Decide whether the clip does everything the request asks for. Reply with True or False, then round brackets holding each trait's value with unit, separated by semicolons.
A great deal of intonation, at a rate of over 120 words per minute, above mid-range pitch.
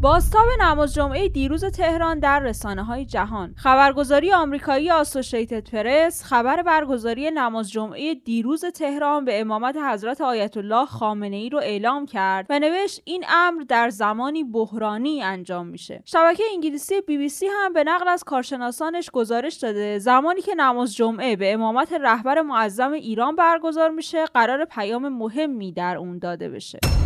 True (5.8 semitones; 150 wpm; 275 Hz)